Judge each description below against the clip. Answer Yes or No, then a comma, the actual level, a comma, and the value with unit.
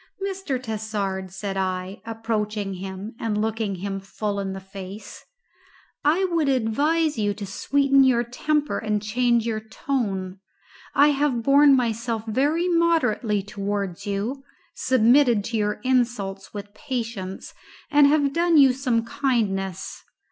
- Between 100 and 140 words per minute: Yes, slow, 135 wpm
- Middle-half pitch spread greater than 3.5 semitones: Yes, average, 5.3 semitones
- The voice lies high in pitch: Yes, high, 225 Hz